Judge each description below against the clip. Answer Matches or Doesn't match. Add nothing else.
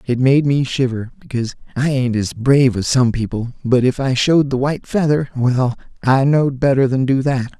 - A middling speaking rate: Matches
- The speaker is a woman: Doesn't match